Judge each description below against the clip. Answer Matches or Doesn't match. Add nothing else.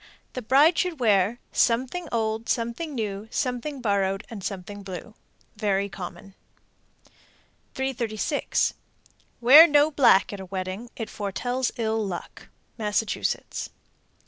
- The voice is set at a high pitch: Matches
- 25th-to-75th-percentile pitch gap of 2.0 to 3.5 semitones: Doesn't match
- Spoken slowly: Matches